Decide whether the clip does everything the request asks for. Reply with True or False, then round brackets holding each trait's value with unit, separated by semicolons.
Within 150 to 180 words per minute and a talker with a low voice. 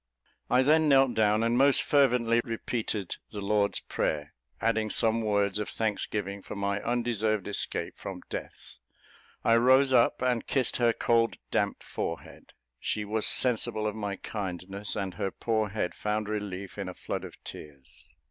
True (155 wpm; 110 Hz)